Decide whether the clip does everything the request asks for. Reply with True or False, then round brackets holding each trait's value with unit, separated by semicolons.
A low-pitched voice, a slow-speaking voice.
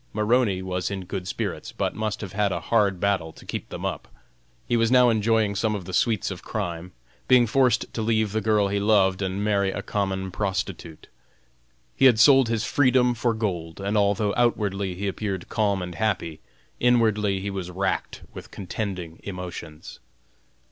False (100 Hz; 175 wpm)